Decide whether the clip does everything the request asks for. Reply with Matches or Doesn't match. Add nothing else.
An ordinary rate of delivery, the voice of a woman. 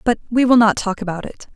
Doesn't match